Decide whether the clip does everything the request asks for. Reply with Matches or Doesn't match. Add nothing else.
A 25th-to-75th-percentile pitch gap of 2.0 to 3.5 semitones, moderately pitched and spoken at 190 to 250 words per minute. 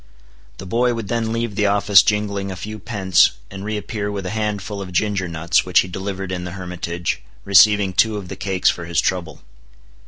Doesn't match